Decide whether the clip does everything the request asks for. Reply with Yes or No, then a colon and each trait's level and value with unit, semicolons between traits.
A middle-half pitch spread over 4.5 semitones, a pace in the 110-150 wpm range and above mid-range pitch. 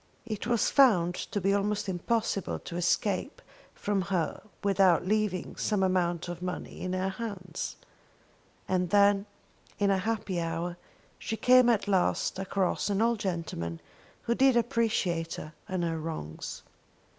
No: average, 3.3 semitones; average, 145 wpm; high, 195 Hz